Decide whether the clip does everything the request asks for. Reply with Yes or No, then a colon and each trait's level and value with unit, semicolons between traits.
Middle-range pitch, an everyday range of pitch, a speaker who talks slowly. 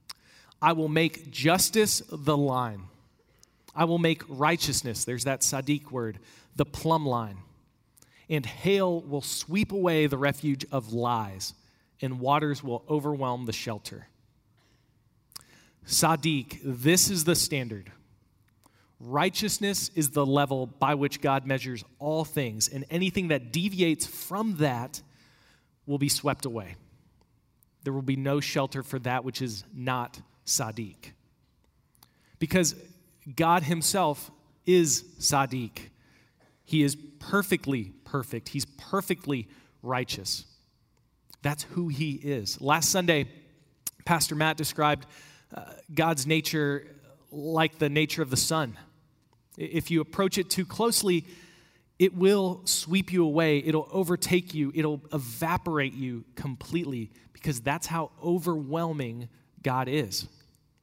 Yes: medium, 145 Hz; average, 4.2 semitones; slow, 120 wpm